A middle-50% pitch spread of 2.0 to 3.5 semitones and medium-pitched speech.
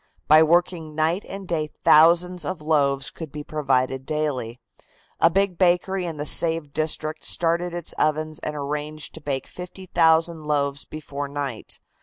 Yes: average, 2.7 semitones; medium, 155 Hz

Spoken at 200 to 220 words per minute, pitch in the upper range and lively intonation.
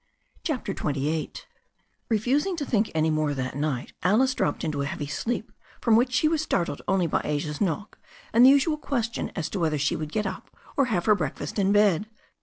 Yes: fast, 205 wpm; high, 195 Hz; wide, 7.8 semitones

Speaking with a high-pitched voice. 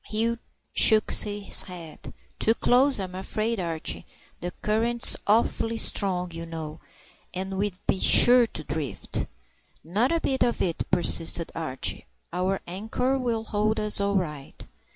Yes: high, 200 Hz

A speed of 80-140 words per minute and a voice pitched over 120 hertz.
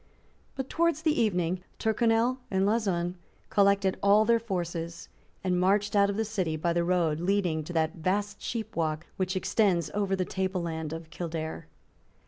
No: average, 160 wpm; medium, 185 Hz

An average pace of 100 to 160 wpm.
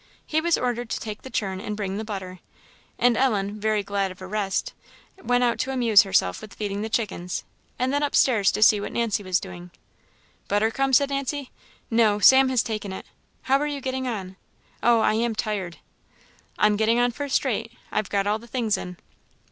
No: fast, 205 wpm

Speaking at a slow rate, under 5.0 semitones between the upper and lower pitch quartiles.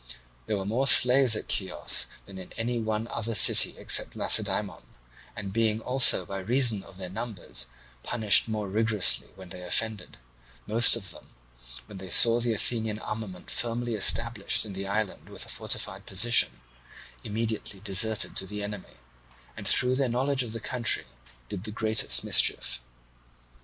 No: average, 155 wpm; average, 3.0 semitones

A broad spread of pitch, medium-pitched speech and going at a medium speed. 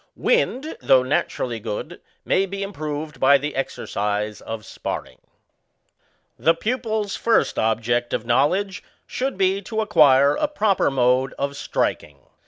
No: wide, 8.3 semitones; medium, 150 Hz; slow, 130 wpm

